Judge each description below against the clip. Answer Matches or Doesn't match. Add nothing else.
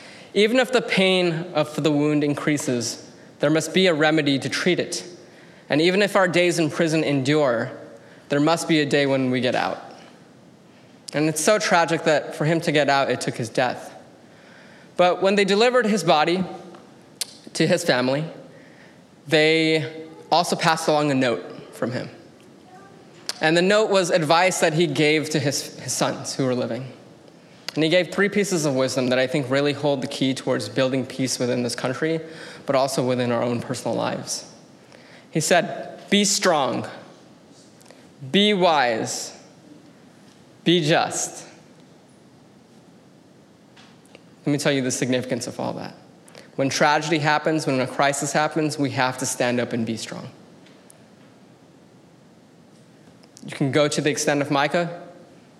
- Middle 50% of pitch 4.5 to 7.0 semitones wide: Doesn't match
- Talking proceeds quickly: Doesn't match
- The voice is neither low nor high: Matches